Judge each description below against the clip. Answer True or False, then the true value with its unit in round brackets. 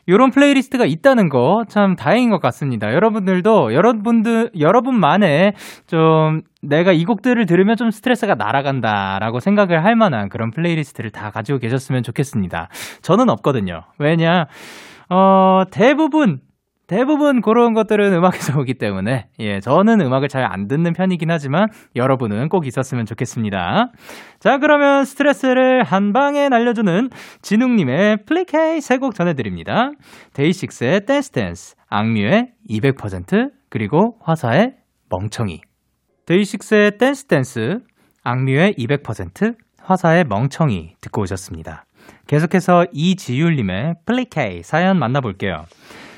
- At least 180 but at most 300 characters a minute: False (315 characters per minute)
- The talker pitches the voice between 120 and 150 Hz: False (175 Hz)